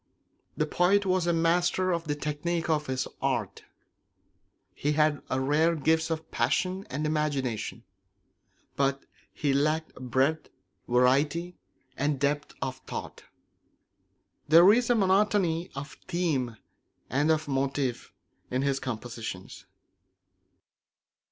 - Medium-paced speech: No, slow, 115 wpm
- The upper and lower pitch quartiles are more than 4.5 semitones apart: No, average, 3.9 semitones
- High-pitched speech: No, medium, 150 Hz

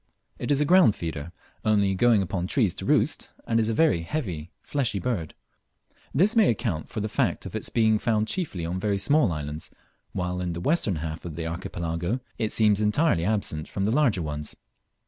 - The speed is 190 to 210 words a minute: Yes, average, 195 wpm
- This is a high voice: No, low, 100 Hz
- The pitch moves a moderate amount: No, wide, 5.8 semitones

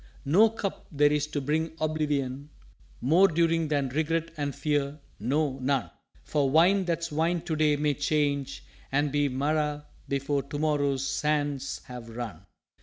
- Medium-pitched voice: Yes, medium, 145 Hz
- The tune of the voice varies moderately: No, narrow, 2.1 semitones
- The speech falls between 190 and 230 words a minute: No, average, 155 wpm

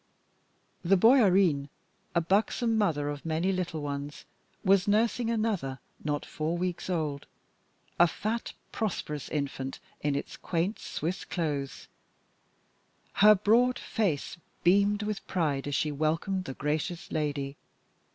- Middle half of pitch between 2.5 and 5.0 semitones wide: No, wide, 5.5 semitones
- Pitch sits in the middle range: Yes, medium, 170 Hz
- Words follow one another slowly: Yes, slow, 120 wpm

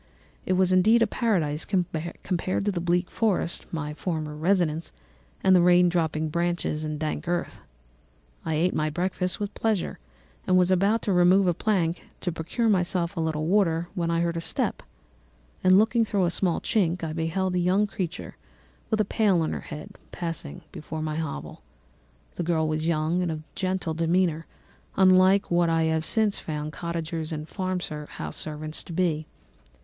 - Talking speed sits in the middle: Yes, average, 170 wpm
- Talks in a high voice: No, medium, 175 Hz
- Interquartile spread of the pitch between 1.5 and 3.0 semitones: Yes, average, 2.7 semitones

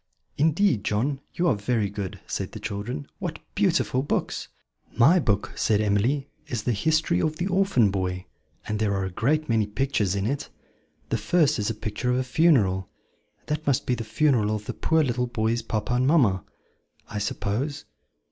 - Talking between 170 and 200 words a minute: Yes, average, 180 wpm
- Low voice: Yes, low, 120 Hz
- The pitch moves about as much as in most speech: No, wide, 5.7 semitones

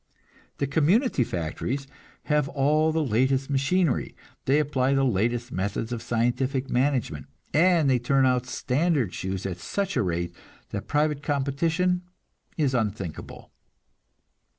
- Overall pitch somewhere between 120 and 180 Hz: Yes, low, 135 Hz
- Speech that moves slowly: Yes, slow, 125 wpm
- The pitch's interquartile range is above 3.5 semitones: Yes, average, 4.0 semitones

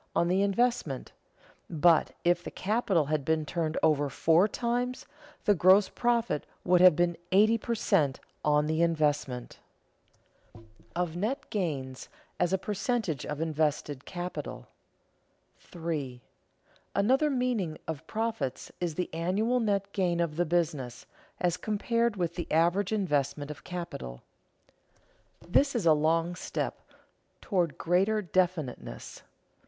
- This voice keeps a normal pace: No, slow, 130 wpm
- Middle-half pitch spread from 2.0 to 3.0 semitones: No, average, 4.7 semitones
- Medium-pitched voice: Yes, medium, 175 Hz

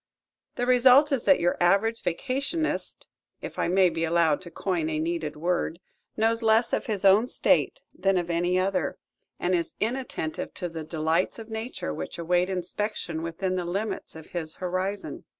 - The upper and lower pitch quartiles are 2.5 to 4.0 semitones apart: No, average, 4.7 semitones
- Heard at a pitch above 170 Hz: Yes, medium, 185 Hz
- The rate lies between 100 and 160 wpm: No, average, 170 wpm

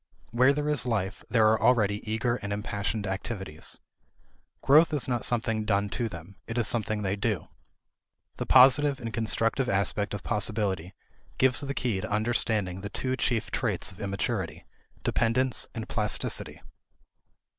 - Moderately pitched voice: No, low, 110 Hz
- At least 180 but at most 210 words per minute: No, average, 150 wpm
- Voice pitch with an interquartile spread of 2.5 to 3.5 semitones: Yes, average, 3.2 semitones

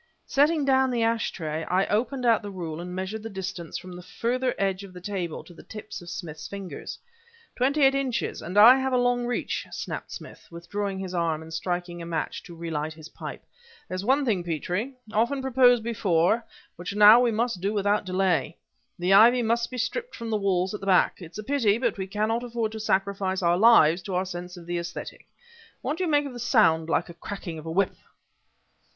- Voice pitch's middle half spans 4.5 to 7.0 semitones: Yes, average, 5.1 semitones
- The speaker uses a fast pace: Yes, fast, 220 wpm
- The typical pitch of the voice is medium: No, high, 200 Hz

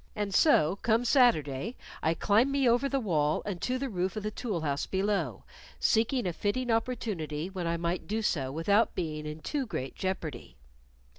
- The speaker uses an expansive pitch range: Yes, wide, 6.5 semitones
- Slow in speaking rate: No, average, 180 wpm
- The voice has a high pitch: Yes, high, 195 Hz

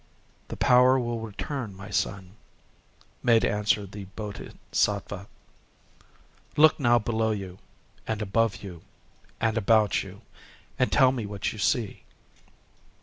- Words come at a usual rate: No, slow, 120 wpm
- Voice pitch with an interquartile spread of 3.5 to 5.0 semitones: No, average, 2.8 semitones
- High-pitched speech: No, low, 110 Hz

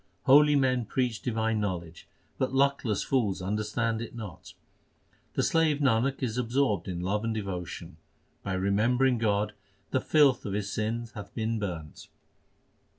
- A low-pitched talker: Yes, low, 110 Hz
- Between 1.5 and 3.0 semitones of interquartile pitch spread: No, average, 4.0 semitones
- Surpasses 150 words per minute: No, average, 145 wpm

